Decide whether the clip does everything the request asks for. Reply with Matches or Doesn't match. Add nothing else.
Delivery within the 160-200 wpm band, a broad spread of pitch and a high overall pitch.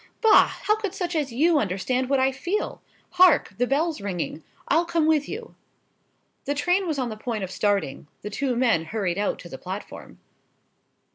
Matches